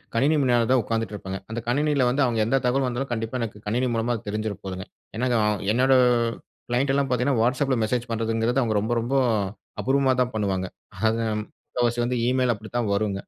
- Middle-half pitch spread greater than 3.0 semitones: No, narrow, 2.5 semitones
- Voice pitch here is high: No, low, 120 Hz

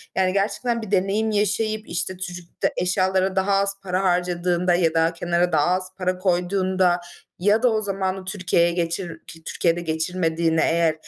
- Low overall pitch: No, medium, 185 Hz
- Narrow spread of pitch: Yes, narrow, 2.2 semitones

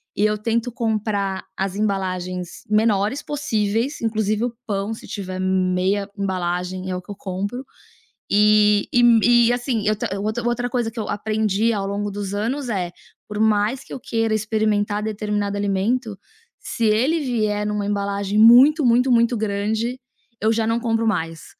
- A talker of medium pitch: No, high, 210 Hz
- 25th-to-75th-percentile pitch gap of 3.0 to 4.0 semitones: No, narrow, 2.5 semitones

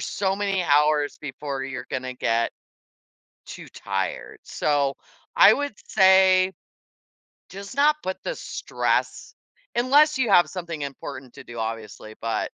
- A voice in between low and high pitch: Yes, medium, 150 Hz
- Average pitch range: No, wide, 7.1 semitones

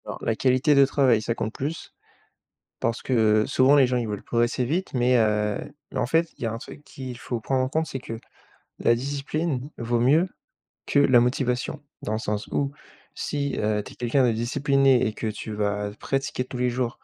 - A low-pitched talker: Yes, low, 125 Hz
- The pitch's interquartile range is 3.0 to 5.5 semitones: Yes, average, 3.3 semitones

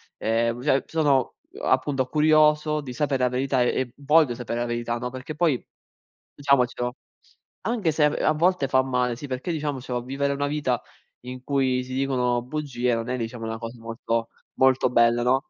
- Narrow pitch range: No, average, 3.0 semitones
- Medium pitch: No, low, 130 Hz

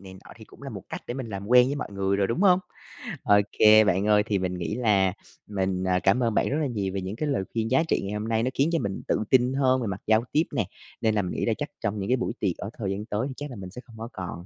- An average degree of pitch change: Yes, average, 4.3 semitones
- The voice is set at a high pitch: No, low, 105 Hz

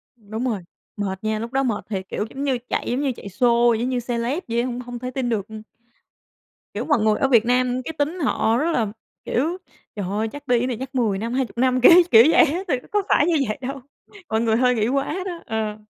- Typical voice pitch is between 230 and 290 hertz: Yes, high, 245 Hz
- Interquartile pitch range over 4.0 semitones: No, average, 3.3 semitones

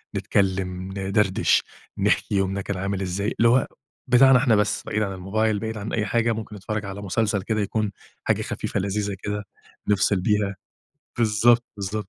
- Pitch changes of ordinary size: No, narrow, 2.0 semitones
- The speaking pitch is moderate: No, low, 105 Hz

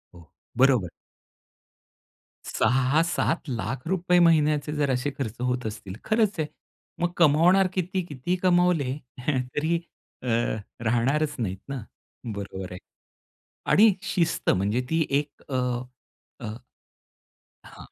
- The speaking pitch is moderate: Yes, medium, 145 Hz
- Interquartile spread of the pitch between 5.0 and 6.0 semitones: Yes, wide, 5.4 semitones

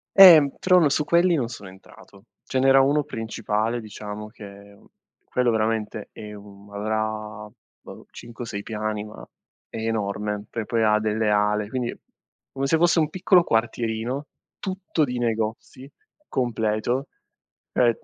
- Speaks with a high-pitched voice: No, low, 110 Hz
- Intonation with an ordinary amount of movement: Yes, average, 3.9 semitones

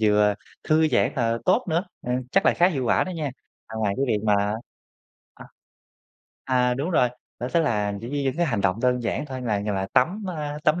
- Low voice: Yes, low, 125 Hz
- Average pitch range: No, wide, 6.2 semitones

